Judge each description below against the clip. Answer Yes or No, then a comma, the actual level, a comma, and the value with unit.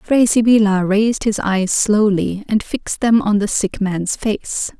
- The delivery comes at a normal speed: Yes, average, 175 wpm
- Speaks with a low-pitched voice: No, high, 210 Hz